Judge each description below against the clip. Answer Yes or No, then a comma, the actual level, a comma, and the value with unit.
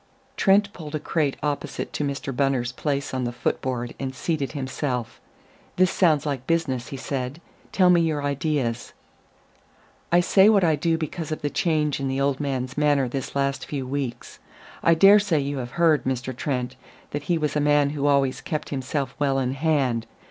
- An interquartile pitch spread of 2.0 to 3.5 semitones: Yes, average, 3.0 semitones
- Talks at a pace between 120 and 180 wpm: No, average, 190 wpm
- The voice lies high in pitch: No, medium, 140 Hz